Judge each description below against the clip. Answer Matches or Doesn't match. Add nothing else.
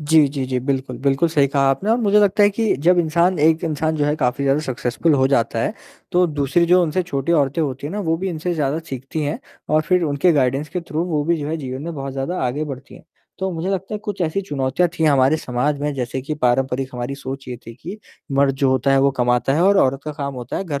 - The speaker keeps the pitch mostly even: Doesn't match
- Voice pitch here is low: Doesn't match